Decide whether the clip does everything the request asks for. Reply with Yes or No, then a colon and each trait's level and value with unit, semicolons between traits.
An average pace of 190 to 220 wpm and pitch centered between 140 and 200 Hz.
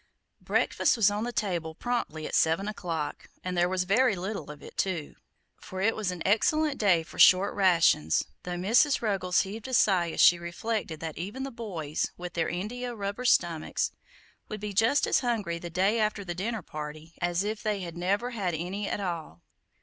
Yes: average, 195 wpm; high, 190 Hz